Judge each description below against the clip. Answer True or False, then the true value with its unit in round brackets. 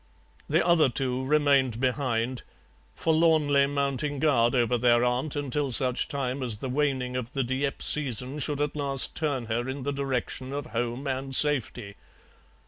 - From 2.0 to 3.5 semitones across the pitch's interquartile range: True (2.5 semitones)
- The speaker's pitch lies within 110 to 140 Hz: True (135 Hz)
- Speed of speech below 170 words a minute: True (155 wpm)